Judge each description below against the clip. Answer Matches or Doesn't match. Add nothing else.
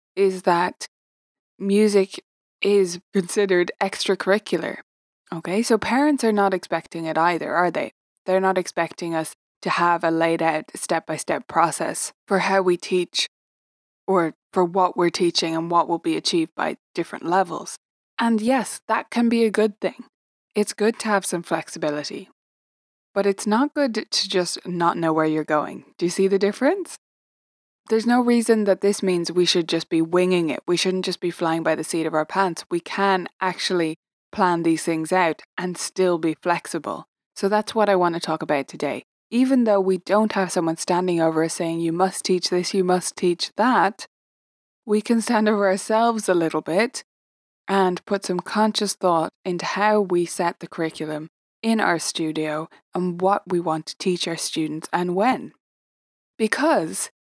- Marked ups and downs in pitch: Doesn't match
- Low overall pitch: Doesn't match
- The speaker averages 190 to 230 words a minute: Doesn't match